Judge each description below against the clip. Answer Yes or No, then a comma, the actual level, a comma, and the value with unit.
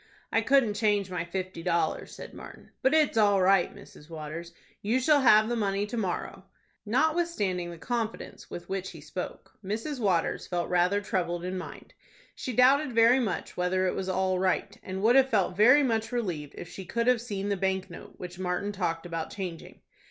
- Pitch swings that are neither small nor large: Yes, average, 4.4 semitones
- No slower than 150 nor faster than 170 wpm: No, average, 190 wpm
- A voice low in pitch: No, high, 195 Hz